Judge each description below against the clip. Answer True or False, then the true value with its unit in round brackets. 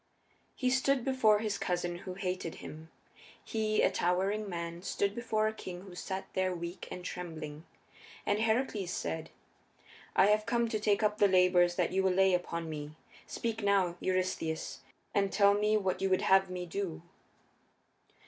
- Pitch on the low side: False (190 Hz)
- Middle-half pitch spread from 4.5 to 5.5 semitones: False (3.1 semitones)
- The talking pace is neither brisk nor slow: True (165 wpm)